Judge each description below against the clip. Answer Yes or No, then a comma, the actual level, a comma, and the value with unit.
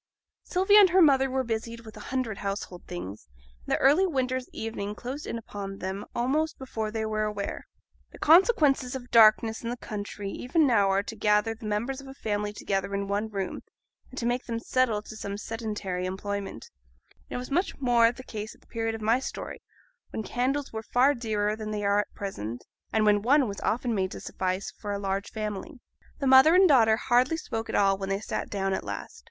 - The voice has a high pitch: Yes, high, 220 Hz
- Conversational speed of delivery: No, fast, 215 wpm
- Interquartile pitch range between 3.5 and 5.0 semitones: Yes, average, 4.1 semitones